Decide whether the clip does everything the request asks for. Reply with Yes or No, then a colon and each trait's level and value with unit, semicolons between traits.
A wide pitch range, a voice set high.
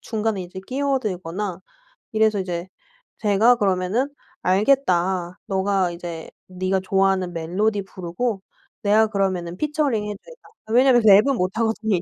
No: average, 3.3 semitones; high, 195 Hz